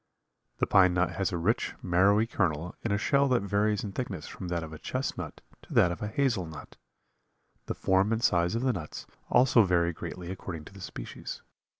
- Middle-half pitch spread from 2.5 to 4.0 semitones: Yes, average, 3.7 semitones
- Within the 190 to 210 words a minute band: Yes, fast, 205 wpm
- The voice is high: No, very low, 95 Hz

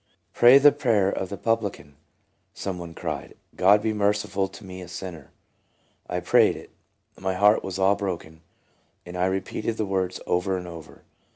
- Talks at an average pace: Yes, average, 185 wpm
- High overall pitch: No, very low, 95 Hz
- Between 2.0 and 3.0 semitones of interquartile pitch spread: Yes, narrow, 2.4 semitones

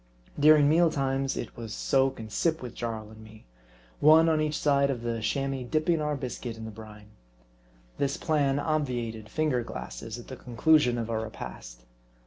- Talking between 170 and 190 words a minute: Yes, average, 175 wpm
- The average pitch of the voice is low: Yes, low, 130 Hz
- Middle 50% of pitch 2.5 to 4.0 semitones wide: No, average, 4.9 semitones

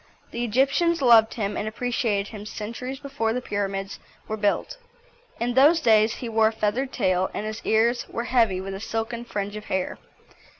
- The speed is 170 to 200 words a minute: Yes, average, 180 wpm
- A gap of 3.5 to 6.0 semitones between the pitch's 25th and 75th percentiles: No, average, 2.9 semitones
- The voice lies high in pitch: Yes, high, 225 Hz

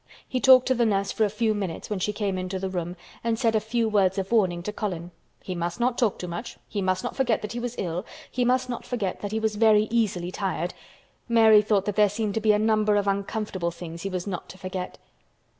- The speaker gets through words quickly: Yes, fast, 250 wpm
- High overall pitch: Yes, high, 210 Hz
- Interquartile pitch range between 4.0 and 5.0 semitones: No, average, 3.2 semitones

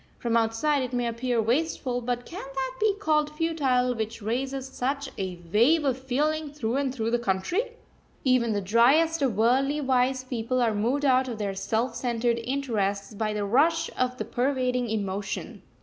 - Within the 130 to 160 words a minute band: No, average, 175 wpm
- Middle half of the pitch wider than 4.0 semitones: No, average, 3.4 semitones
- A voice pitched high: Yes, very high, 250 Hz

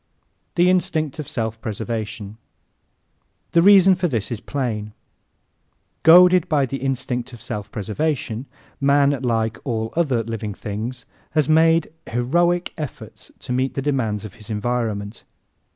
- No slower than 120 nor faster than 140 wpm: Yes, slow, 135 wpm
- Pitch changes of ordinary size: No, wide, 5.7 semitones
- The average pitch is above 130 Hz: No, low, 125 Hz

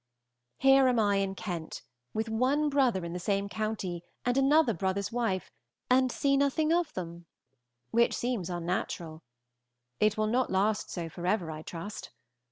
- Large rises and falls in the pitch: Yes, wide, 6.1 semitones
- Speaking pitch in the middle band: No, high, 215 Hz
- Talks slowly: No, average, 155 wpm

